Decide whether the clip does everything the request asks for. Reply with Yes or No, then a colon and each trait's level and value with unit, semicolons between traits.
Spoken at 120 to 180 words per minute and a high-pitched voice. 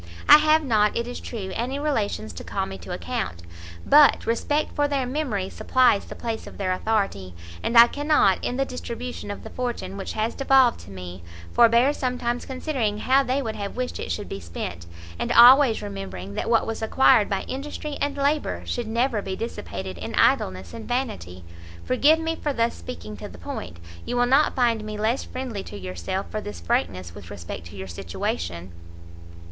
No: average, 190 wpm; high, 225 Hz